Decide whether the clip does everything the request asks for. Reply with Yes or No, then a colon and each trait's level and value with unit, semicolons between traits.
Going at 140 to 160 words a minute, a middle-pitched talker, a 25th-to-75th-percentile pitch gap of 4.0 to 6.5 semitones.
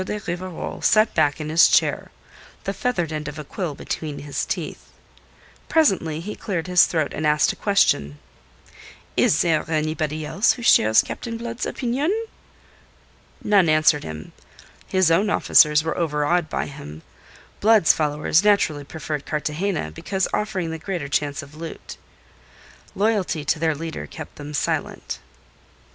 Yes: average, 145 wpm; medium, 160 Hz; average, 4.6 semitones